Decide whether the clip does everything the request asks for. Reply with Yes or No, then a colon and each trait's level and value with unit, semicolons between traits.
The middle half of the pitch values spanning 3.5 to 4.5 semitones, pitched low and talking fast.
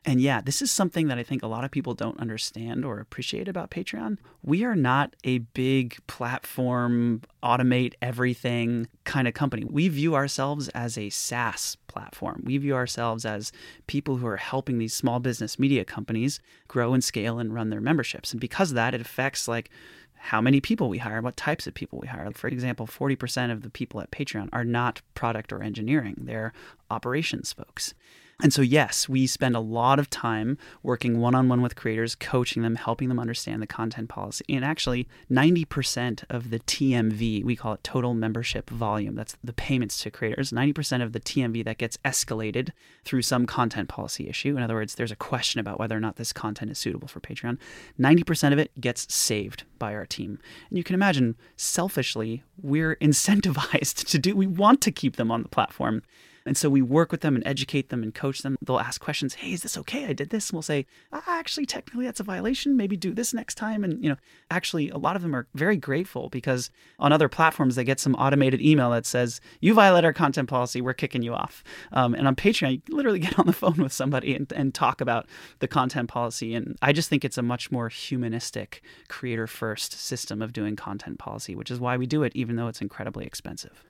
Yes: average, 3.9 semitones; low, 125 Hz; fast, 210 wpm